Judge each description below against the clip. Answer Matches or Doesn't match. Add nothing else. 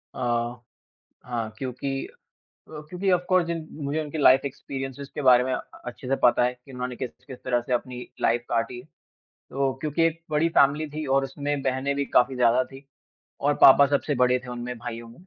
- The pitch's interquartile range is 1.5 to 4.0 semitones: Matches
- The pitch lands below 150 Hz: Matches